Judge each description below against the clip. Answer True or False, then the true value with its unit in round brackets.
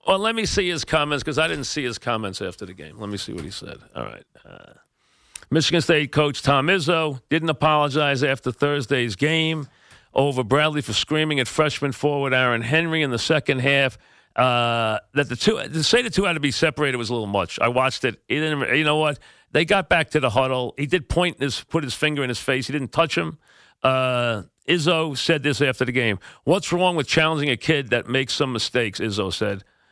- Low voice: False (145 Hz)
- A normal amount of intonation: True (3.8 semitones)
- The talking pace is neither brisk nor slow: False (220 wpm)